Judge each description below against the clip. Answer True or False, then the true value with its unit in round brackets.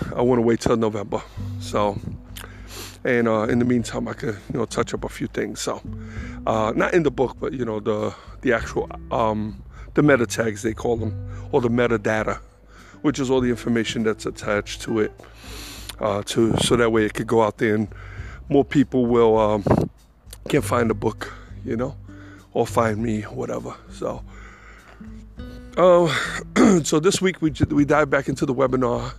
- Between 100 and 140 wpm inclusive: False (185 wpm)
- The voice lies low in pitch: True (110 Hz)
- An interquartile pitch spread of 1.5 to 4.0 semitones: True (2.8 semitones)